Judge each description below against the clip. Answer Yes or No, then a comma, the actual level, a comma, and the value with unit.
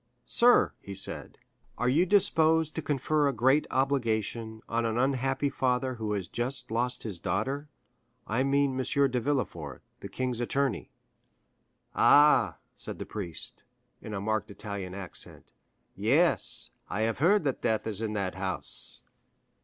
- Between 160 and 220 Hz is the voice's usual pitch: No, low, 120 Hz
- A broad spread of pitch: No, average, 4.8 semitones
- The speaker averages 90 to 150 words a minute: Yes, average, 145 wpm